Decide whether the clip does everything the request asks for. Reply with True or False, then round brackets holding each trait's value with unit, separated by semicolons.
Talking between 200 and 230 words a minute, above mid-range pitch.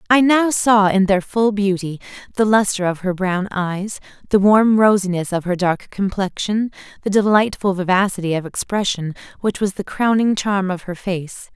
False (170 wpm; 195 Hz)